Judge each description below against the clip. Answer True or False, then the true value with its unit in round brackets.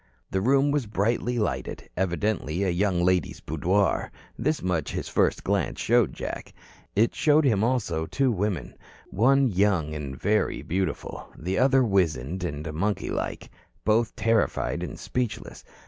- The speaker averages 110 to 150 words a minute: True (145 wpm)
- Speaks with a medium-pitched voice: False (100 Hz)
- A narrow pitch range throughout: False (5.2 semitones)